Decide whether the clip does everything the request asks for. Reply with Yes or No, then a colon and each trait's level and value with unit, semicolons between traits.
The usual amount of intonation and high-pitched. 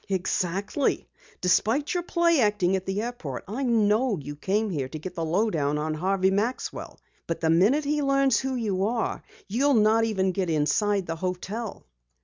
Yes: average, 4.8 semitones; high, 200 Hz